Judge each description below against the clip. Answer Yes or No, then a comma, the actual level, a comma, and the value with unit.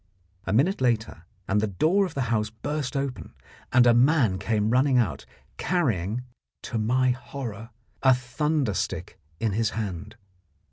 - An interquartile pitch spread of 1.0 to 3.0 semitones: No, average, 4.2 semitones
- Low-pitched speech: Yes, low, 120 Hz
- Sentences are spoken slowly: No, average, 150 wpm